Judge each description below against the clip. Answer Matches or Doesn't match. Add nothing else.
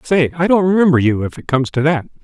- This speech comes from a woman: Doesn't match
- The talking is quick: Matches